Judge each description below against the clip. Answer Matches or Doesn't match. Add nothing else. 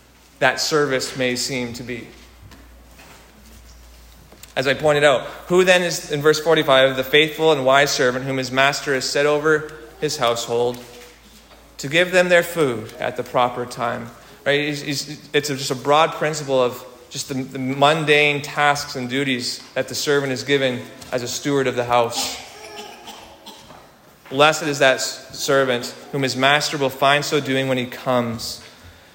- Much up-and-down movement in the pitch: Doesn't match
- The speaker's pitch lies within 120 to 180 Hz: Matches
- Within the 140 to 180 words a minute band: Matches